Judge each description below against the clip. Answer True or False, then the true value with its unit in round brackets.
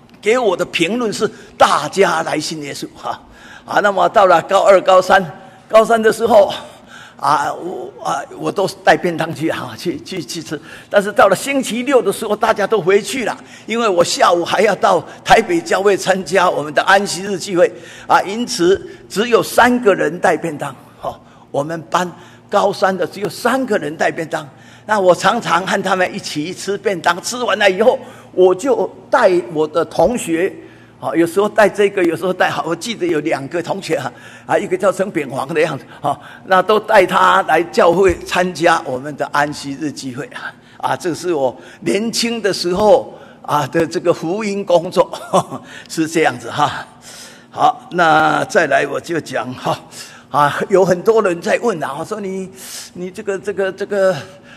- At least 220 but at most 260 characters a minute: True (255 characters per minute)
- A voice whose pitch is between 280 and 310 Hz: False (190 Hz)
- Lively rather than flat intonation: False (4.5 semitones)